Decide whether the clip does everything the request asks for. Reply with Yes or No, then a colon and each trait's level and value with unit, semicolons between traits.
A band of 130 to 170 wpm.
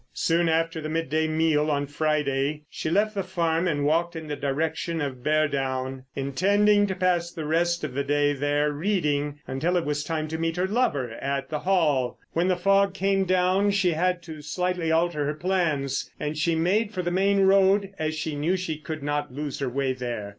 No: average, 200 wpm